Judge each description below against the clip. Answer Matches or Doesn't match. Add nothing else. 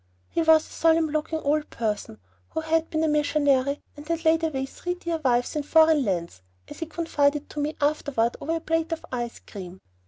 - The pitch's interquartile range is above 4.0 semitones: Doesn't match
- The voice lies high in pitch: Matches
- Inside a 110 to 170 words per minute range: Doesn't match